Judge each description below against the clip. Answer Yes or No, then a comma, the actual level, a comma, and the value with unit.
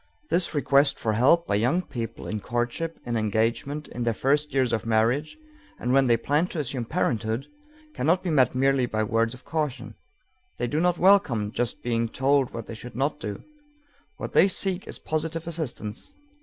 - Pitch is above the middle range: No, low, 130 Hz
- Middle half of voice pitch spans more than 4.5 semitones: Yes, average, 4.9 semitones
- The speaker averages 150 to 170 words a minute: No, average, 185 wpm